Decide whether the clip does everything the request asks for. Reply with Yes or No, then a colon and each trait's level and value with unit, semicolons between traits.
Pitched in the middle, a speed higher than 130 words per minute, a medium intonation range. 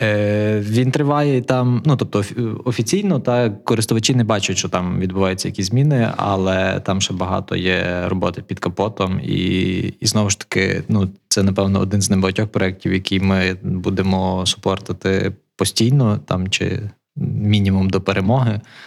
No: low, 100 Hz; average, 145 wpm; average, 3.3 semitones